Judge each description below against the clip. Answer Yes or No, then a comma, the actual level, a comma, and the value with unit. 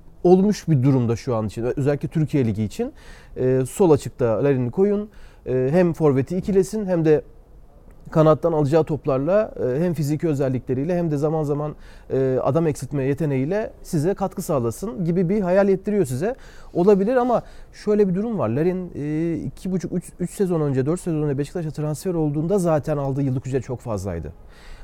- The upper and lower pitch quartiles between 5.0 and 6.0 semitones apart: Yes, wide, 5.4 semitones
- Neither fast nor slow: No, fast, 155 wpm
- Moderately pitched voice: Yes, medium, 155 Hz